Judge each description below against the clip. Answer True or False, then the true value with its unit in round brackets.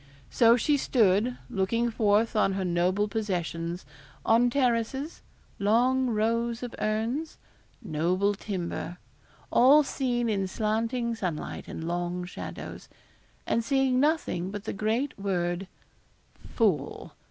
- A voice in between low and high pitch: False (220 Hz)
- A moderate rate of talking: False (115 wpm)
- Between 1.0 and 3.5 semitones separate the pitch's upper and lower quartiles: False (4.4 semitones)